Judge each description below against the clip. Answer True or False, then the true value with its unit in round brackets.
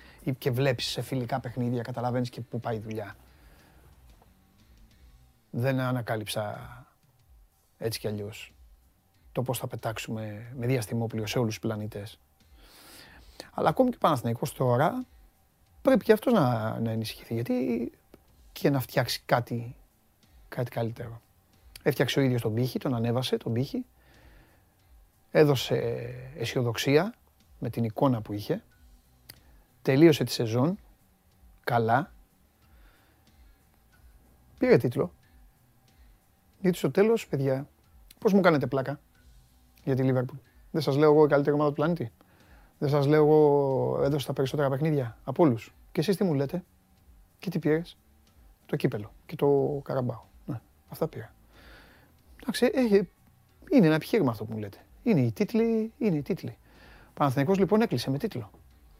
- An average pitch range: False (6.0 semitones)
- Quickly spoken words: False (135 wpm)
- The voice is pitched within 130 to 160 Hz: False (120 Hz)